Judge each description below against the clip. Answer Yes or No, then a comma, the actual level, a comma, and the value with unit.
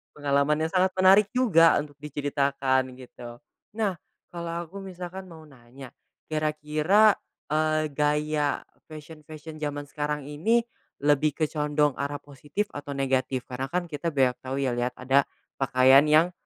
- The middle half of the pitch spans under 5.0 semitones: Yes, average, 3.0 semitones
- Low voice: No, medium, 150 Hz